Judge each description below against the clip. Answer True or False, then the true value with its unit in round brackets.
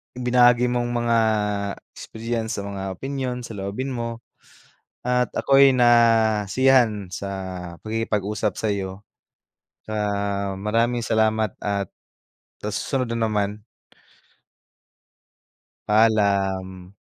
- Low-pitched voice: True (110 Hz)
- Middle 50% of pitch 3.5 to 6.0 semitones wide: False (3.0 semitones)